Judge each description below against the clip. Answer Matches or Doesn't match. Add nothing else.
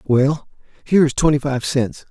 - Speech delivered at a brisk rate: Doesn't match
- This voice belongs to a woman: Doesn't match